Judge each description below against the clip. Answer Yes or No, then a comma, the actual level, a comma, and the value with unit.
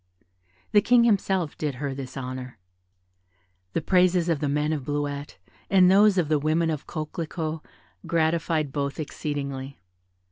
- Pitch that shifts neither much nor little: Yes, average, 3.2 semitones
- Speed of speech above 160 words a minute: No, average, 140 wpm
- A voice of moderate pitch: Yes, medium, 155 Hz